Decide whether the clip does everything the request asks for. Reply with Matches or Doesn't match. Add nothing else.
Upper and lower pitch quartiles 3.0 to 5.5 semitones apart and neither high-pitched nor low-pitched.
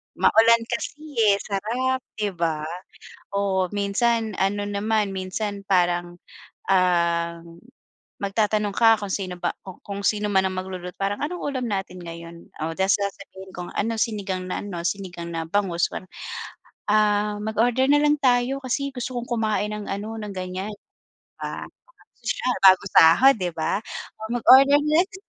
Doesn't match